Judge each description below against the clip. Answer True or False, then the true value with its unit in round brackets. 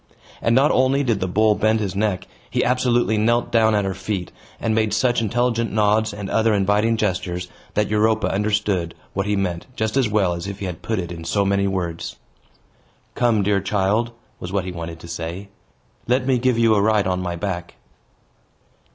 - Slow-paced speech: False (195 wpm)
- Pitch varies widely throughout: False (3.0 semitones)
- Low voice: True (105 Hz)